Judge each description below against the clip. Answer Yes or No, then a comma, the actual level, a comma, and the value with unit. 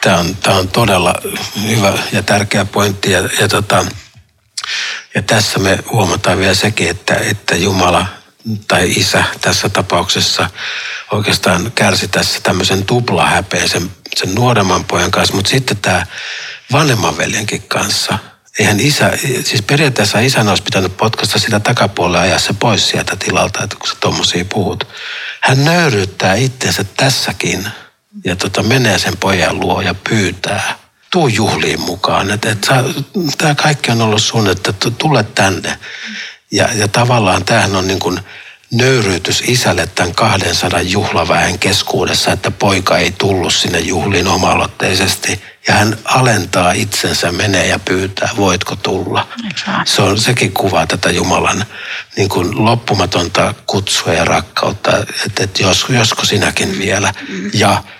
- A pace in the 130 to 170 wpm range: Yes, average, 135 wpm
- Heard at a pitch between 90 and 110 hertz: Yes, low, 100 Hz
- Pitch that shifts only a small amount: No, average, 3.4 semitones